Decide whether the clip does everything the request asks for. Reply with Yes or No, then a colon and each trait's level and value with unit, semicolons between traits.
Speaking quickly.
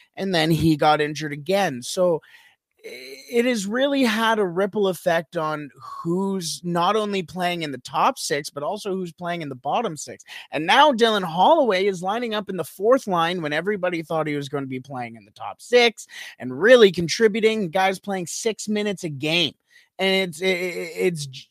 No: average, 190 wpm